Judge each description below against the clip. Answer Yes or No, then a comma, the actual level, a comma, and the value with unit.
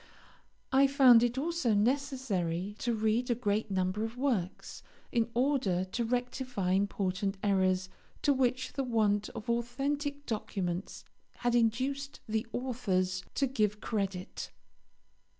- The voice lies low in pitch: No, high, 230 Hz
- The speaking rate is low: Yes, slow, 125 wpm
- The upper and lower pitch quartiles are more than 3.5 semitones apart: Yes, average, 4.7 semitones